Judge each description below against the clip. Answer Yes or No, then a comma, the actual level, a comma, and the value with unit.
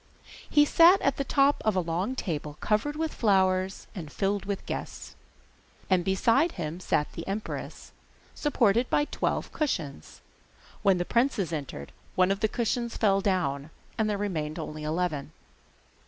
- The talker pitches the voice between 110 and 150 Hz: No, high, 195 Hz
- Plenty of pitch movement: Yes, wide, 6.0 semitones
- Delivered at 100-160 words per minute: Yes, average, 155 wpm